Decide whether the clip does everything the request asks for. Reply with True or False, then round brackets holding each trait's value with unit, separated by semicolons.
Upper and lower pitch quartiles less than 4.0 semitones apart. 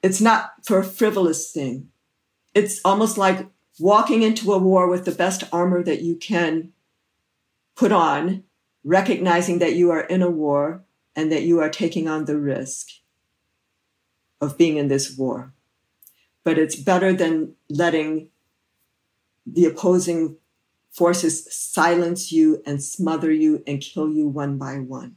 True (3.4 semitones)